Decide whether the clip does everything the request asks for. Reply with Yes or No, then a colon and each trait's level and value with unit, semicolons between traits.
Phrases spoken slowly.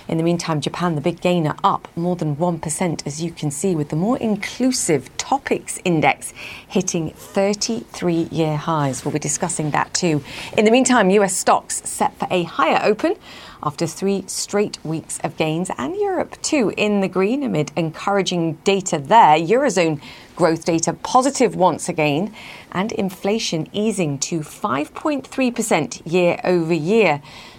No: average, 150 wpm